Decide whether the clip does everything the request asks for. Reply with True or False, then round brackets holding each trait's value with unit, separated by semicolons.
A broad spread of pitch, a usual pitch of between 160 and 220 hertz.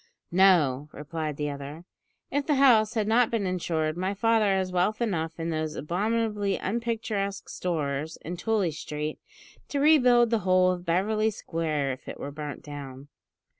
True (5.9 semitones; 185 Hz)